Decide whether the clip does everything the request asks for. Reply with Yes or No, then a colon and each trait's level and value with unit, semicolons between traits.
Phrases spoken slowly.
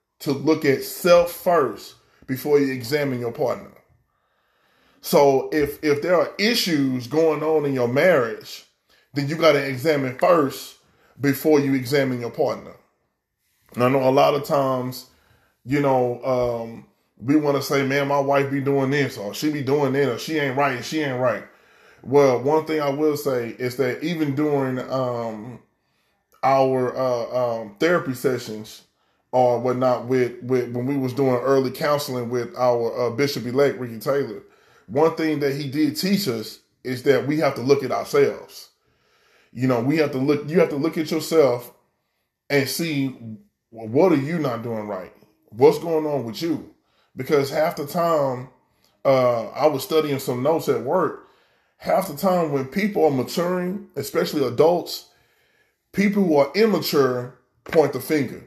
No: average, 170 wpm